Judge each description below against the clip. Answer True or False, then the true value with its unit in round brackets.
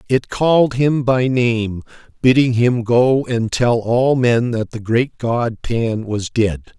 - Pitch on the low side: True (120 Hz)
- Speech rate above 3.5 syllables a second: False (3.4 syllables/s)